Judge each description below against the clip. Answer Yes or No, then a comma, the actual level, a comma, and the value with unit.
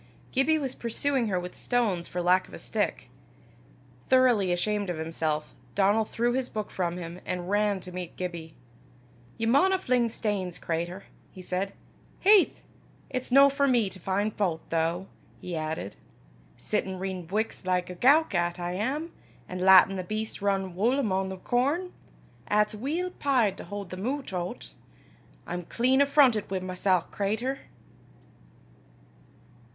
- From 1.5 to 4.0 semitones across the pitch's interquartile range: No, average, 5.3 semitones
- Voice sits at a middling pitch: No, high, 200 Hz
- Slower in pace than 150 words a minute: No, average, 155 wpm